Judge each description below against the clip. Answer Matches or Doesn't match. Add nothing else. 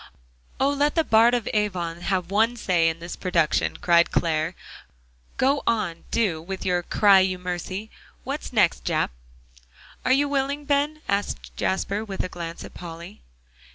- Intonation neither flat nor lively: Doesn't match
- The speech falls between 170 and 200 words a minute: Doesn't match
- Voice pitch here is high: Matches